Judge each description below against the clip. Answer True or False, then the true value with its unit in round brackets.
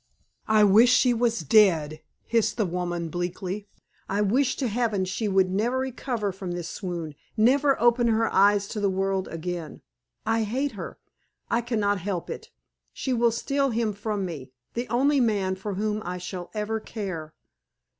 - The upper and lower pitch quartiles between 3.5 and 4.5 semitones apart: True (4.0 semitones)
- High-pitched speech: True (210 Hz)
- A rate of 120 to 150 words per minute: False (170 wpm)